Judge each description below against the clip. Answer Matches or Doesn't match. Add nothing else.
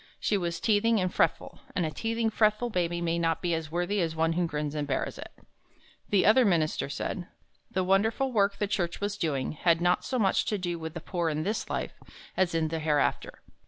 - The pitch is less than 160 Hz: Doesn't match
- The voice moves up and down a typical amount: Matches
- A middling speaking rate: Doesn't match